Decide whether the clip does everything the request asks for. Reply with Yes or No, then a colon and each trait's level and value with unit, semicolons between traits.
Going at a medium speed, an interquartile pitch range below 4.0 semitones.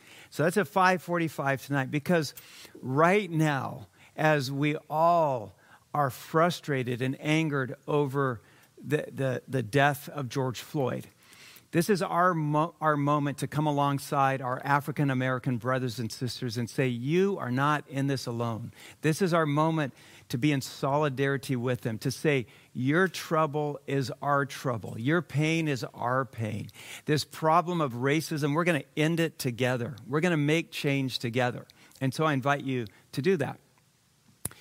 Yes: average, 160 wpm; average, 3.3 semitones